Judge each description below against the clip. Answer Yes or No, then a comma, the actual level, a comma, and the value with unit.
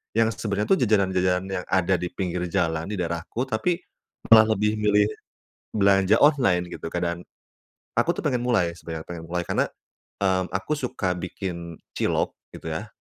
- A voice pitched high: No, very low, 95 Hz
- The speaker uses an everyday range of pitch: Yes, average, 3.4 semitones